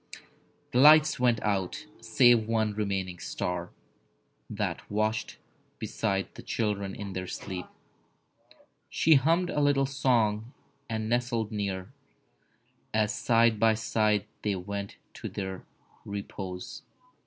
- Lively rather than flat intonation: No, average, 3.2 semitones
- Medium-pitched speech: No, low, 110 Hz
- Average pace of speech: No, slow, 115 wpm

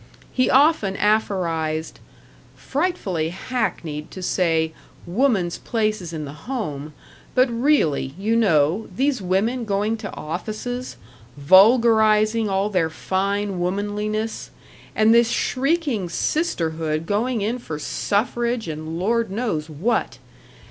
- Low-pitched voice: No, high, 205 Hz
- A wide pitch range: Yes, wide, 5.8 semitones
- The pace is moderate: No, slow, 115 wpm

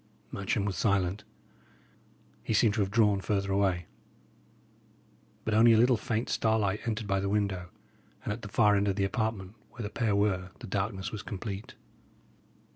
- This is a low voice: Yes, low, 105 Hz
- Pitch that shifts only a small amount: Yes, narrow, 2.1 semitones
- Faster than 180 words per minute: No, average, 170 wpm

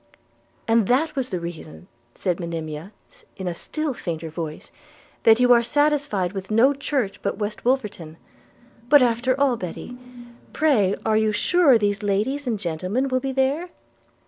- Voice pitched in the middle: No, high, 220 Hz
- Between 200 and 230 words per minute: No, average, 155 wpm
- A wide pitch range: Yes, wide, 6.4 semitones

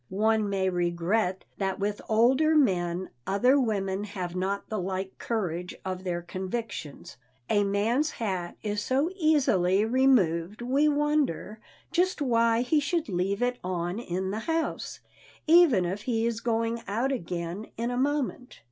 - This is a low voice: No, high, 215 Hz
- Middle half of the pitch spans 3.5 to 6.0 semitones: Yes, average, 5.2 semitones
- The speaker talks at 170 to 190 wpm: No, average, 150 wpm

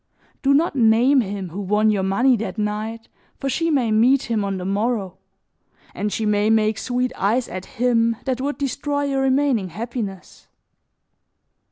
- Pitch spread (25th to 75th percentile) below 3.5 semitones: No, average, 4.0 semitones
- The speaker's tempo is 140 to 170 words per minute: Yes, average, 165 wpm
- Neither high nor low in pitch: No, high, 225 Hz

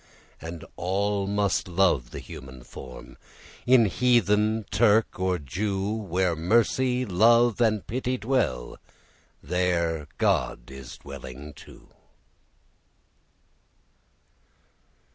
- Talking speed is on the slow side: Yes, slow, 90 wpm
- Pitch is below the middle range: Yes, very low, 95 Hz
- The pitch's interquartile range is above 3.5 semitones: Yes, wide, 5.4 semitones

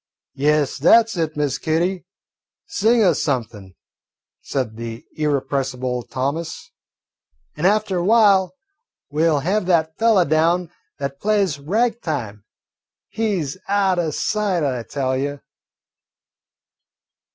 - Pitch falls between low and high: Yes, medium, 160 Hz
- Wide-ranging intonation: Yes, wide, 5.9 semitones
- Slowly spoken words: Yes, slow, 120 wpm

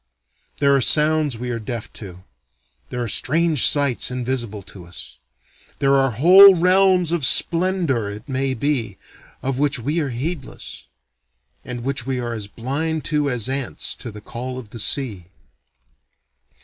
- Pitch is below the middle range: Yes, low, 130 Hz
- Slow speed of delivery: No, average, 155 wpm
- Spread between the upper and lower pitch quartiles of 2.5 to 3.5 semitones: No, average, 4.3 semitones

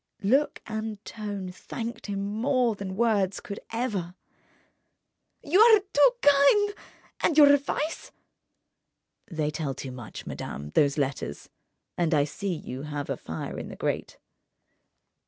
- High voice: Yes, high, 200 Hz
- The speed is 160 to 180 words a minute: No, slow, 135 wpm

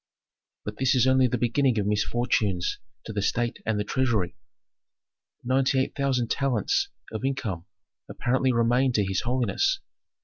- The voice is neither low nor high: No, low, 120 Hz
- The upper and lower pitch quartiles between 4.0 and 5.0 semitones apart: No, average, 3.5 semitones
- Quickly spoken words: No, average, 145 wpm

